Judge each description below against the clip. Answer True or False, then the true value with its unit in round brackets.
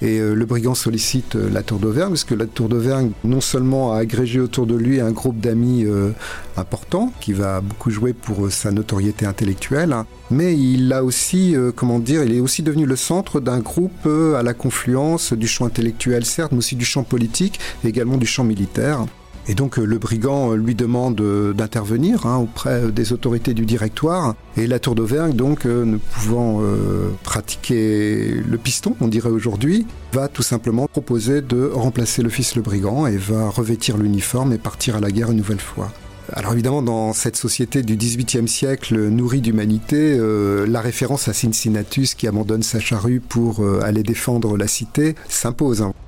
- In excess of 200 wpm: False (180 wpm)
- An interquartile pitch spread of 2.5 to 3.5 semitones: True (2.8 semitones)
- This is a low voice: True (120 Hz)